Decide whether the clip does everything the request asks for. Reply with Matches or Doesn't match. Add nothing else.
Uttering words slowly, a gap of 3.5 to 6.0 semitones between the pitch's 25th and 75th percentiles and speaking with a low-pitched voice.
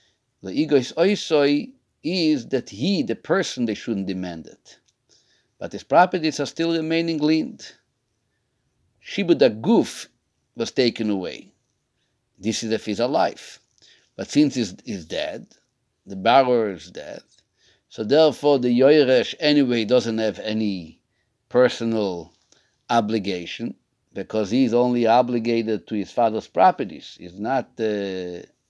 Matches